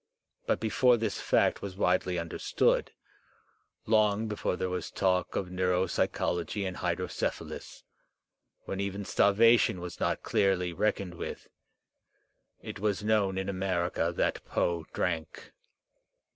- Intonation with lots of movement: No, narrow, 2.4 semitones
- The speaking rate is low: Yes, slow, 115 wpm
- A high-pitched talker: No, very low, 95 Hz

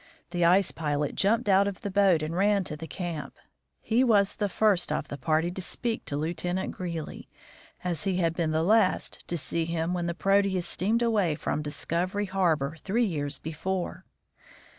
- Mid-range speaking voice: Yes, medium, 175 Hz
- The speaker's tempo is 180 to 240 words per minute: Yes, average, 185 wpm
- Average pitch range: Yes, average, 3.6 semitones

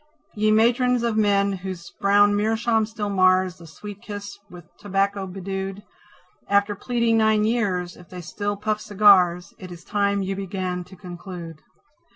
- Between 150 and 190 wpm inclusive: Yes, average, 155 wpm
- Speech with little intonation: Yes, narrow, 2.3 semitones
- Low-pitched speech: No, high, 200 Hz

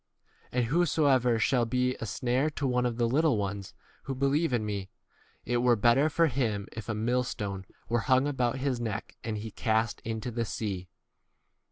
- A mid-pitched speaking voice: No, low, 120 Hz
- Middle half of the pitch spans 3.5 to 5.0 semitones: No, average, 3.0 semitones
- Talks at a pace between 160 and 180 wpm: No, average, 195 wpm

